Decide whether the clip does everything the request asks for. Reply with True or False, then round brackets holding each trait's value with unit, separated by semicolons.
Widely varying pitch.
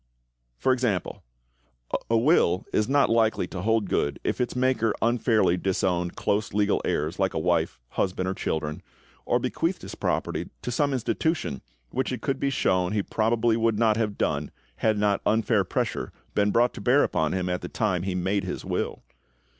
False (4.2 semitones)